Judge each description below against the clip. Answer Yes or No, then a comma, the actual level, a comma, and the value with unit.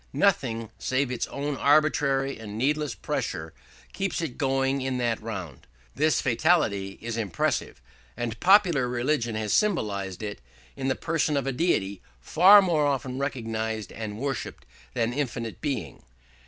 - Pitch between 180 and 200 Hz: No, low, 130 Hz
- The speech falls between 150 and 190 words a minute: No, average, 140 wpm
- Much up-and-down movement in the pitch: No, average, 4.8 semitones